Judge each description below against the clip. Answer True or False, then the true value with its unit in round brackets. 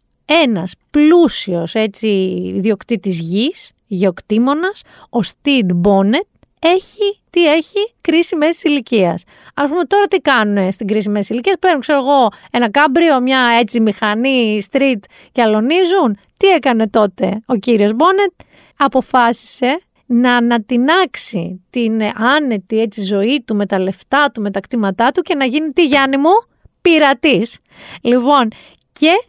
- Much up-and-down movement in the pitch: True (6.5 semitones)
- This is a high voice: True (245 Hz)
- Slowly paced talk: False (135 wpm)